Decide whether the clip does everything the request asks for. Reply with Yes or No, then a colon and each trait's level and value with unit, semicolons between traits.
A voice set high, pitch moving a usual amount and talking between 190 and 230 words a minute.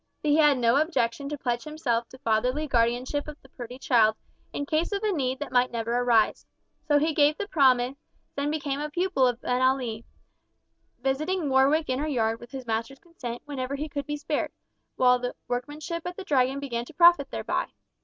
Yes: very high, 270 Hz; average, 3.5 semitones; average, 195 wpm